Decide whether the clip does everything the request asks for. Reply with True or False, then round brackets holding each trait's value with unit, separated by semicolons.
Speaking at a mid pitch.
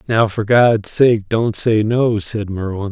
False (110 Hz)